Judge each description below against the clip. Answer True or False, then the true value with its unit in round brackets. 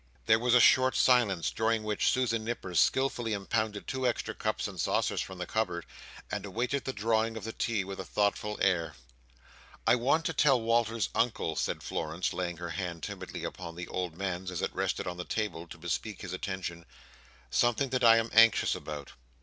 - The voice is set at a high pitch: False (110 Hz)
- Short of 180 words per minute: False (190 wpm)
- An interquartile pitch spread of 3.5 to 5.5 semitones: True (4.4 semitones)